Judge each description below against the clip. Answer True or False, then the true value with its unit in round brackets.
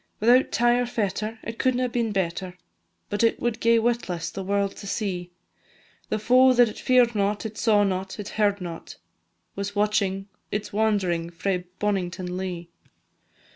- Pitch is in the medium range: False (205 Hz)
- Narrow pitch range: False (3.5 semitones)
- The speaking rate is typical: True (160 wpm)